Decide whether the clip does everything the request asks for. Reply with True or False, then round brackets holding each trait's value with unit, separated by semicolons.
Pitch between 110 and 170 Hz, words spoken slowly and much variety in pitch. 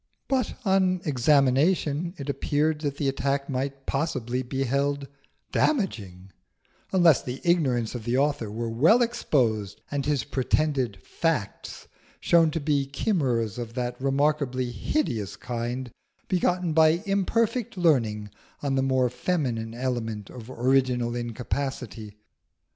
False (135 Hz; 125 wpm; 4.5 semitones)